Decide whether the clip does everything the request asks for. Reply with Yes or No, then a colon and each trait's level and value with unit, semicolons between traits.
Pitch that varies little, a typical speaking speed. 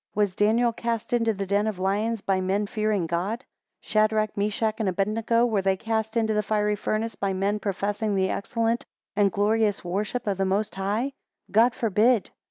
Yes: narrow, 2.2 semitones; average, 180 wpm